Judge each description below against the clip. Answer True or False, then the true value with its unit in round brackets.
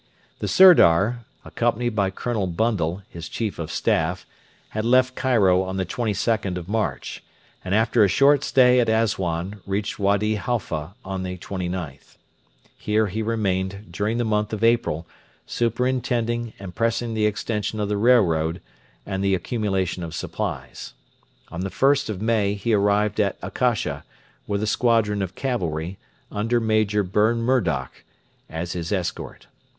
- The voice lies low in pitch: True (105 Hz)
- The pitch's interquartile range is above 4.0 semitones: False (3.7 semitones)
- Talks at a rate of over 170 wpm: False (145 wpm)